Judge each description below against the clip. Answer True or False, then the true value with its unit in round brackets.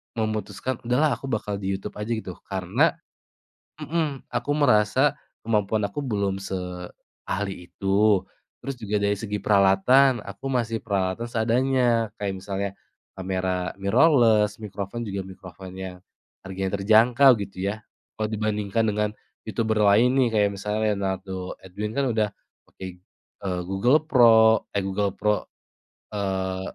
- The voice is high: False (105 Hz)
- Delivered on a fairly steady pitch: False (3.0 semitones)